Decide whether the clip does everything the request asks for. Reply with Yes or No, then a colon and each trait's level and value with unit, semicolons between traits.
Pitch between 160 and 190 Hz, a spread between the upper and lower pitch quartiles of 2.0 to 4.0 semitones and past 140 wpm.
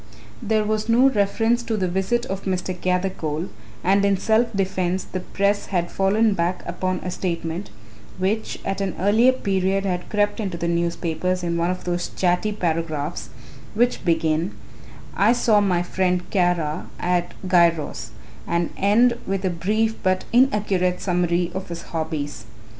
Yes: medium, 185 Hz; average, 2.9 semitones; average, 155 wpm